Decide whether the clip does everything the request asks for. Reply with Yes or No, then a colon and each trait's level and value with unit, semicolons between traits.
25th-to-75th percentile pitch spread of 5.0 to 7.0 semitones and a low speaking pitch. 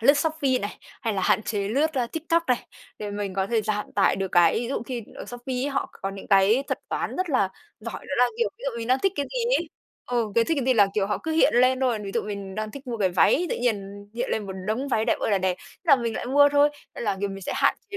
No: average, 5.3 semitones; high, 235 Hz